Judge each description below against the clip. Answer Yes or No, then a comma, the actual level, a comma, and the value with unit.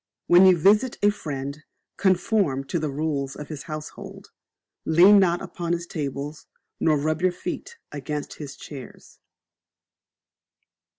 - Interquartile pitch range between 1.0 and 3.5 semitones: No, average, 3.9 semitones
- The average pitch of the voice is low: No, medium, 155 Hz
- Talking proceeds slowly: Yes, slow, 130 wpm